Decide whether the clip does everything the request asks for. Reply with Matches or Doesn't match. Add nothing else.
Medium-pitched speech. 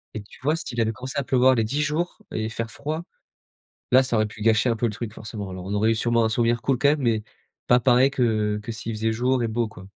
Doesn't match